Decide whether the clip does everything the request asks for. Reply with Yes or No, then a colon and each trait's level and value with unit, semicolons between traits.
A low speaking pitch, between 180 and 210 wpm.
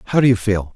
No: low, 110 Hz; fast, 320 wpm